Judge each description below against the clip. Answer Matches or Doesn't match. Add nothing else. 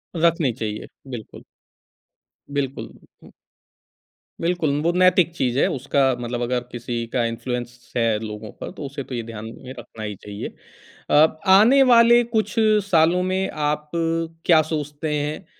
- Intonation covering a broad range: Matches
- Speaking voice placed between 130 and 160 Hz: Matches